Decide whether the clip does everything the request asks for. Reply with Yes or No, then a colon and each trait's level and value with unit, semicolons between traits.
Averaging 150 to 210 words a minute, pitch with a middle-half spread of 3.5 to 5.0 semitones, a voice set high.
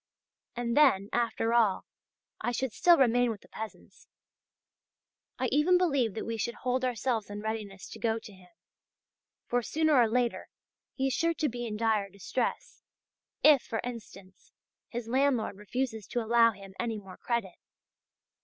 No: average, 160 wpm; average, 2.9 semitones; high, 235 Hz